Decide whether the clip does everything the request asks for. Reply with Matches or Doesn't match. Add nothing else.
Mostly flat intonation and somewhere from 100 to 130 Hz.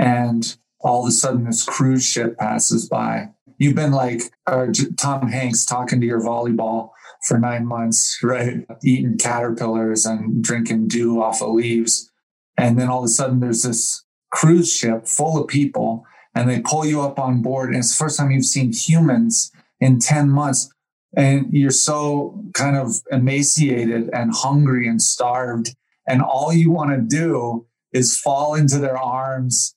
Doesn't match